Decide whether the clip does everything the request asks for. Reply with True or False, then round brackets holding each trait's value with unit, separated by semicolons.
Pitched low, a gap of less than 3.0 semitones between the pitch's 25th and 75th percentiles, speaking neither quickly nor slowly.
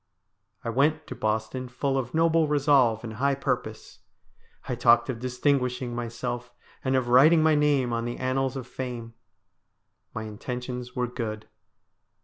True (125 Hz; 2.5 semitones; 145 wpm)